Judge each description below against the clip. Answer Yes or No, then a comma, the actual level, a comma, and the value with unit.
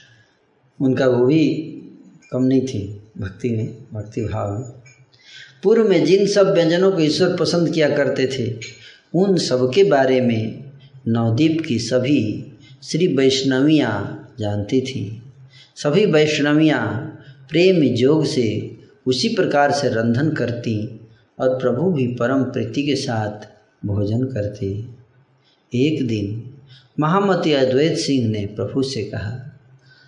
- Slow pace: No, average, 125 wpm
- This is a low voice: Yes, low, 130 Hz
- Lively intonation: No, average, 4.2 semitones